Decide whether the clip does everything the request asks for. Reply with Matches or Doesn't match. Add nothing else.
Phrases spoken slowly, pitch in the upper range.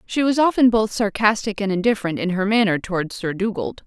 Doesn't match